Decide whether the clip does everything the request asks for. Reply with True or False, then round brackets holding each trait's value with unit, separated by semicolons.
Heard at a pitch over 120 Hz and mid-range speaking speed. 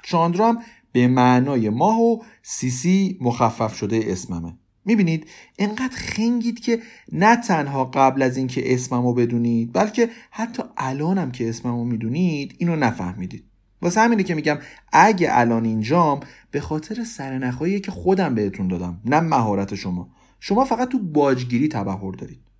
True (140 Hz; 140 wpm)